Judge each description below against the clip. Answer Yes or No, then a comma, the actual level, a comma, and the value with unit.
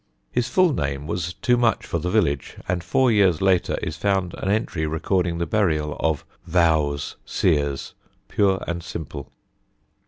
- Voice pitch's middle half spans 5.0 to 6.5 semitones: No, average, 4.1 semitones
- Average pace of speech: Yes, average, 155 wpm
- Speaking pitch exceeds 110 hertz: No, very low, 85 Hz